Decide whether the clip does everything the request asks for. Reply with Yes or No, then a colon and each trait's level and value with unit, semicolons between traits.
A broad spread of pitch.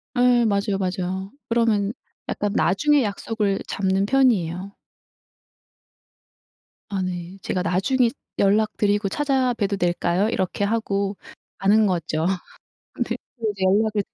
No: average, 2.9 semitones